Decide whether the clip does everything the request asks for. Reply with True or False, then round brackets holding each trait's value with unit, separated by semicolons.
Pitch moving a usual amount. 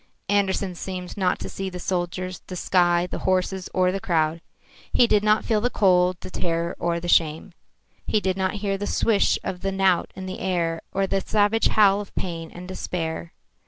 False (2.0 semitones)